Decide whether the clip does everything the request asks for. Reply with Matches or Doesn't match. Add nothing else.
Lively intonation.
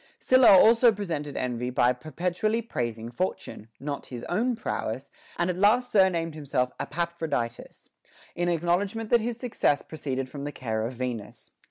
Matches